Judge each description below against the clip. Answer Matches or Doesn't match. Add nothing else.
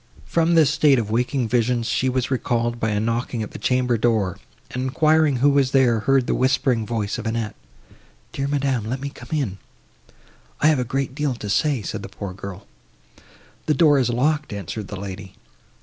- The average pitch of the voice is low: Matches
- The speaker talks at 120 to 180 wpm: Doesn't match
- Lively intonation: Doesn't match